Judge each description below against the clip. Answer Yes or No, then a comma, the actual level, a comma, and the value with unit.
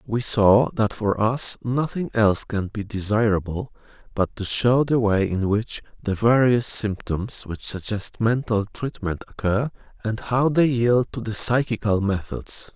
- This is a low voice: Yes, low, 110 Hz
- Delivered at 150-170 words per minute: Yes, average, 155 wpm